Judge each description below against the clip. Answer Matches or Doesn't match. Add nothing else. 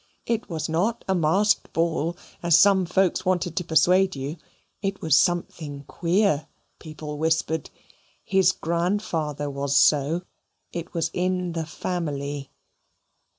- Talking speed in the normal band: Doesn't match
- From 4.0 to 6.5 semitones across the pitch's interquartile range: Doesn't match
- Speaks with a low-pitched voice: Doesn't match